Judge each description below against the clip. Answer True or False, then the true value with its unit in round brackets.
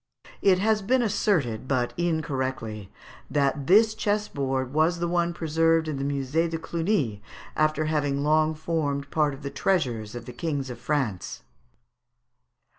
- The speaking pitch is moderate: True (155 Hz)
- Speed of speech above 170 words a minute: False (145 wpm)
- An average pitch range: True (4.1 semitones)